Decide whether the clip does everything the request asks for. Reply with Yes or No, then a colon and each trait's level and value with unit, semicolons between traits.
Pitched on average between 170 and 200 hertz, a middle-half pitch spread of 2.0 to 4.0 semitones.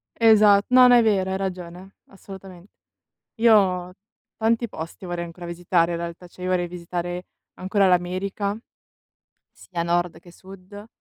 Yes: medium, 185 Hz; narrow, 2.4 semitones